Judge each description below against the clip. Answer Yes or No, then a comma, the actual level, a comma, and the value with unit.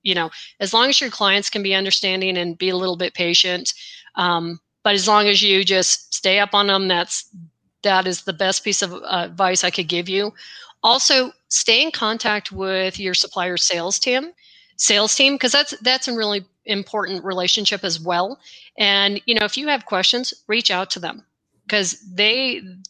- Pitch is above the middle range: Yes, high, 195 Hz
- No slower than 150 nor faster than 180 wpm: No, average, 190 wpm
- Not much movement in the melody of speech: No, average, 3.1 semitones